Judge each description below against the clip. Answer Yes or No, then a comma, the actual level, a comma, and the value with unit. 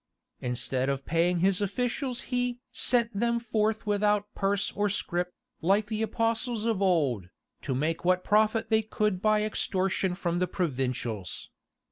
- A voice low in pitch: No, high, 200 Hz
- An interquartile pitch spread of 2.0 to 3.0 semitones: No, average, 4.2 semitones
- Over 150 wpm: No, average, 145 wpm